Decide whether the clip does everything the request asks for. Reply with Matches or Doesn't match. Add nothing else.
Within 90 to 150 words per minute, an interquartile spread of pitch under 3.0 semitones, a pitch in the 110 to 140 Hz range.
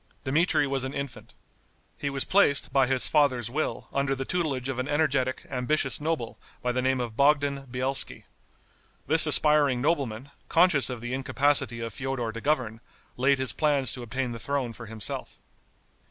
Doesn't match